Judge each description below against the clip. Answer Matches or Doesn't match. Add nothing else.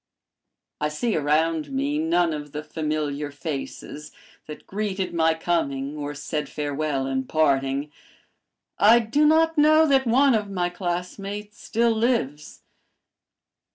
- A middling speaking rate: Doesn't match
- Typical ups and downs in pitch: Doesn't match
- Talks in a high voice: Doesn't match